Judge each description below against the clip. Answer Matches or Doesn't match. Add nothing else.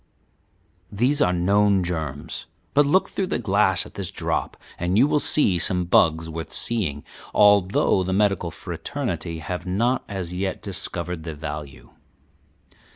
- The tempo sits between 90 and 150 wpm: Matches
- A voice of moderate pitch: Doesn't match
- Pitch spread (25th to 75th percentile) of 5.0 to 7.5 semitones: Doesn't match